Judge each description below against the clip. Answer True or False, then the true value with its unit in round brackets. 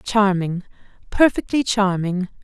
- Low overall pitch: False (200 Hz)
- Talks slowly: True (75 wpm)